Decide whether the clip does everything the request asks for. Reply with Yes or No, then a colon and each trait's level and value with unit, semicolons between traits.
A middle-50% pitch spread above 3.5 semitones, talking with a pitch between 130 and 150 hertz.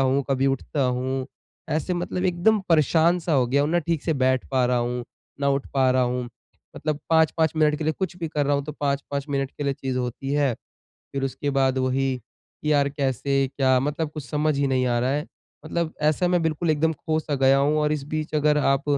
No: average, 2.7 semitones; medium, 140 Hz